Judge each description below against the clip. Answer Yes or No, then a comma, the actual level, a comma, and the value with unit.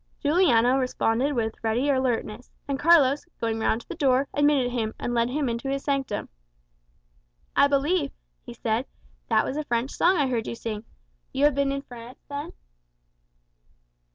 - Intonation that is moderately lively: Yes, average, 3.4 semitones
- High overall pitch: Yes, very high, 260 Hz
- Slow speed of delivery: No, average, 165 wpm